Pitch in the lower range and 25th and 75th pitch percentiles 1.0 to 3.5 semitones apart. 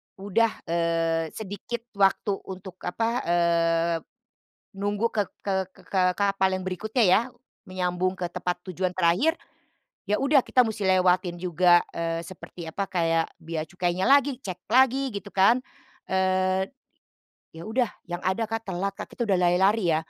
No: medium, 185 Hz; average, 3.2 semitones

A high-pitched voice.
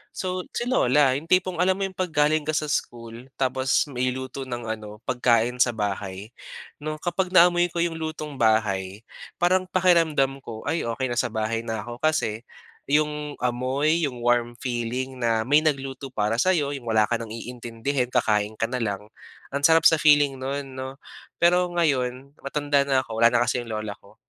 No: low, 130 Hz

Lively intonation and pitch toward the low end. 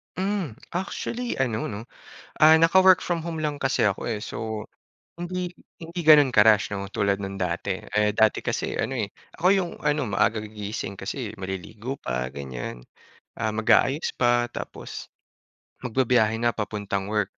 Yes: wide, 7.3 semitones; low, 110 Hz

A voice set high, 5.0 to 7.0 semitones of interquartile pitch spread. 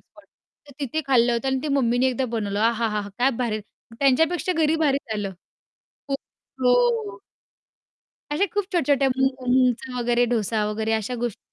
No: high, 245 Hz; average, 3.3 semitones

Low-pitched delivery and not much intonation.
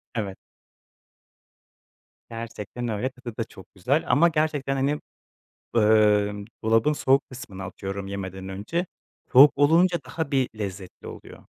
No: low, 115 Hz; wide, 5.5 semitones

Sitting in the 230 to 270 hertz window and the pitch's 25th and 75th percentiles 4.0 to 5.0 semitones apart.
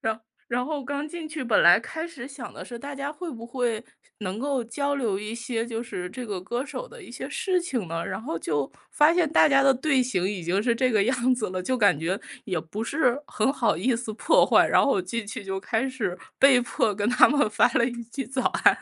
Yes: high, 240 Hz; average, 4.6 semitones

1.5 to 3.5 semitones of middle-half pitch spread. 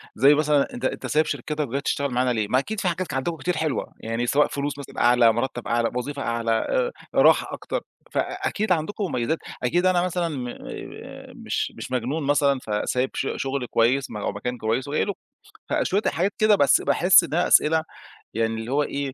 No: average, 4.7 semitones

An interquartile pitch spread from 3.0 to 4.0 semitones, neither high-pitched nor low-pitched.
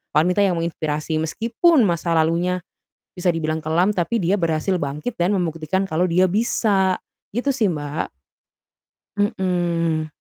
Yes: average, 3.4 semitones; medium, 175 Hz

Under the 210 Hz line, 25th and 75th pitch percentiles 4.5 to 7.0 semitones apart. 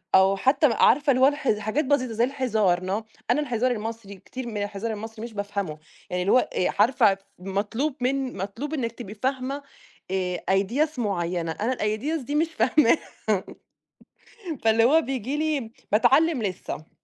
No: high, 230 Hz; average, 5.0 semitones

